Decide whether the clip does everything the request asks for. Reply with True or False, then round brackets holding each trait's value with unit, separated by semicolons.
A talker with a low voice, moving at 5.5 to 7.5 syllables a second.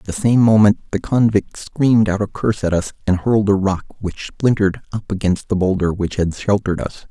True (100 Hz; 5.7 syllables/s)